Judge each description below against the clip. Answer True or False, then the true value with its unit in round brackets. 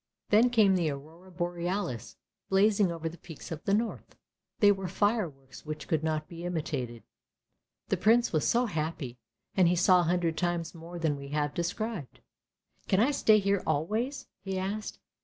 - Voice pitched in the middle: True (175 Hz)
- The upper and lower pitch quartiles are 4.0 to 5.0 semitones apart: True (4.3 semitones)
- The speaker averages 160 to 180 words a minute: True (175 wpm)